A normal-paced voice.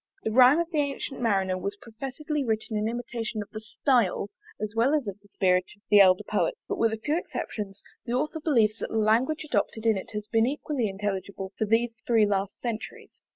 No: fast, 210 wpm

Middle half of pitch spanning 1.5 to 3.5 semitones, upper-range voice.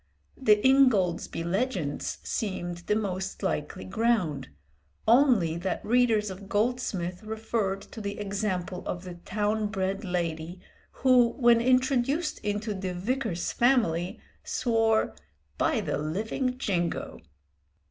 No: average, 4.7 semitones; high, 205 Hz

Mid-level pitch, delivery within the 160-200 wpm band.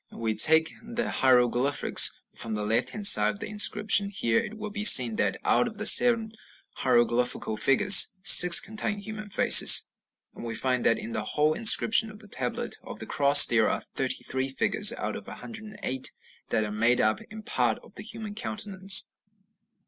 Yes: medium, 160 Hz; average, 175 wpm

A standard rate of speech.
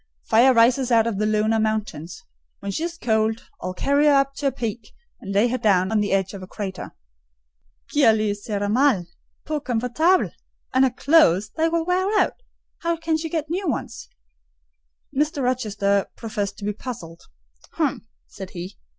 Yes: average, 175 wpm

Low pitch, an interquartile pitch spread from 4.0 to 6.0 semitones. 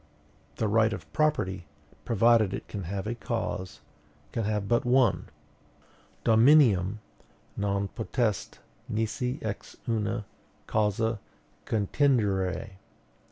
No: low, 110 Hz; average, 2.8 semitones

